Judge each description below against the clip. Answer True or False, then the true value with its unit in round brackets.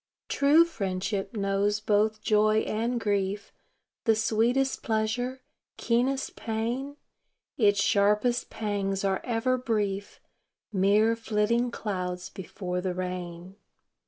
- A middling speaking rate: False (100 wpm)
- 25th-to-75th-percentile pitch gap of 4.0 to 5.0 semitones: False (3.1 semitones)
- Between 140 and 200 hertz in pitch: False (215 Hz)